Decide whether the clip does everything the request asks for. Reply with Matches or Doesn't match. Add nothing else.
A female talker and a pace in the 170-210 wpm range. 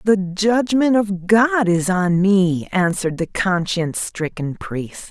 Doesn't match